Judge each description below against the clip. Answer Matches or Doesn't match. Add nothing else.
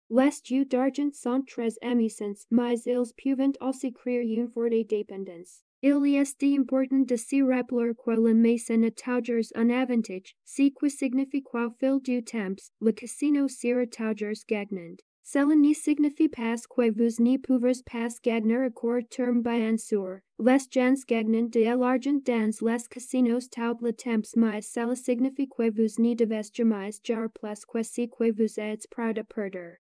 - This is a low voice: Doesn't match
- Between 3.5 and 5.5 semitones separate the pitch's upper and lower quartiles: Doesn't match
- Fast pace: Doesn't match